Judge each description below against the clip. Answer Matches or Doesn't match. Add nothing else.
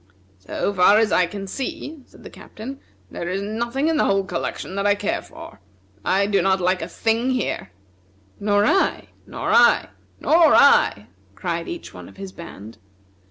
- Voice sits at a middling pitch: Doesn't match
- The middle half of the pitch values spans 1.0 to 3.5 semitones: Doesn't match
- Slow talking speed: Doesn't match